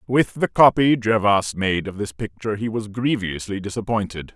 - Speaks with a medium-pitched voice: No, low, 105 Hz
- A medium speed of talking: Yes, average, 165 wpm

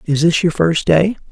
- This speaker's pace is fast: Yes, fast, 230 wpm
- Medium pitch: Yes, medium, 170 Hz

